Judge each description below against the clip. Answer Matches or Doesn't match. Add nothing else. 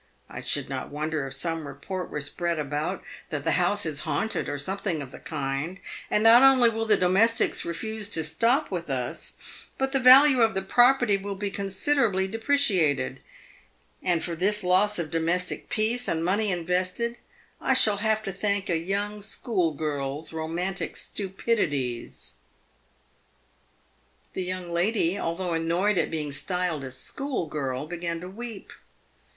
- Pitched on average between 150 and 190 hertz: Matches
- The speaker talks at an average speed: Matches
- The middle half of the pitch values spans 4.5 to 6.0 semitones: Matches